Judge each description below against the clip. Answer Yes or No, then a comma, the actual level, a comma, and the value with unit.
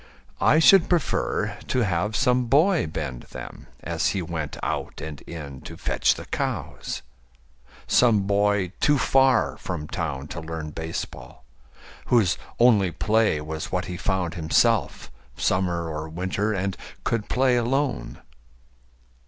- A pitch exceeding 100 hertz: No, very low, 95 Hz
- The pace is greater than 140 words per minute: No, slow, 135 wpm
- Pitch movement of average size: No, wide, 6.7 semitones